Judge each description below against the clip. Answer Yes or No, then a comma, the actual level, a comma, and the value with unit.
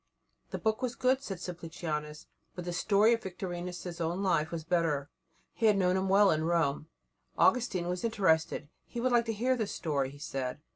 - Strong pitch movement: No, average, 4.8 semitones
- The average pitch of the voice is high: No, medium, 180 Hz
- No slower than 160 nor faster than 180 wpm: No, average, 190 wpm